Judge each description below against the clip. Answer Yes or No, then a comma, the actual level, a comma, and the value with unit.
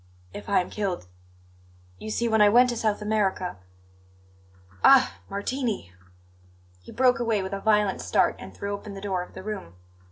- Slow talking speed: No, average, 170 wpm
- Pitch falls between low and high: No, high, 210 Hz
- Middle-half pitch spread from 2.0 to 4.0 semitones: Yes, average, 2.7 semitones